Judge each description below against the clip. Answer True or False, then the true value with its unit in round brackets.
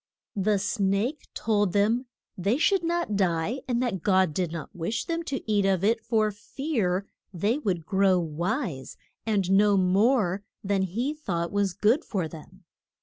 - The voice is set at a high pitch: True (200 Hz)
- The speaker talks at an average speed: True (160 wpm)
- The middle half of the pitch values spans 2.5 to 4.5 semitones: True (4.0 semitones)